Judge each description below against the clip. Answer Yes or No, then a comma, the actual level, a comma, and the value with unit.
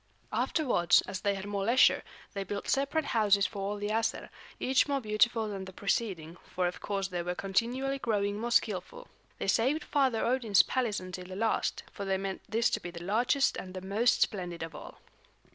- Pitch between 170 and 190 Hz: No, high, 205 Hz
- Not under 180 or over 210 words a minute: Yes, average, 195 wpm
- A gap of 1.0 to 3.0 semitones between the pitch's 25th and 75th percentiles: No, average, 3.9 semitones